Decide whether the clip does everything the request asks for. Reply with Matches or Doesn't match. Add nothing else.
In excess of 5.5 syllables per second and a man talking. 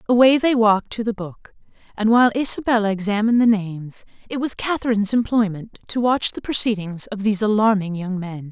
Doesn't match